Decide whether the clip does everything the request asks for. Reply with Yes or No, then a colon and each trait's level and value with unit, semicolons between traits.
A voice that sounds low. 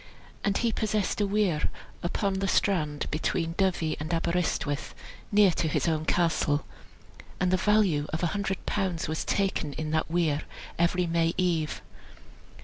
No: medium, 175 Hz